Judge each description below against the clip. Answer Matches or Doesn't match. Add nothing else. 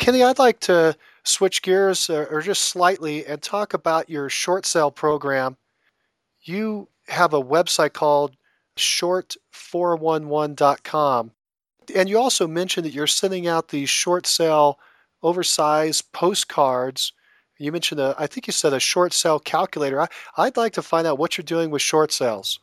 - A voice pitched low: Doesn't match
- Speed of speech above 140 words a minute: Matches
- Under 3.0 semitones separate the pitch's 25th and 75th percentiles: Doesn't match